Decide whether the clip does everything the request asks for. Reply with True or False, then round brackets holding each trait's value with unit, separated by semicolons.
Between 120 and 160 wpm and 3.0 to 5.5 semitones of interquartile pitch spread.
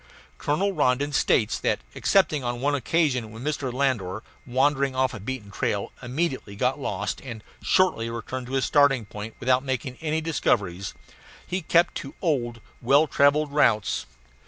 True (155 wpm; 3.9 semitones)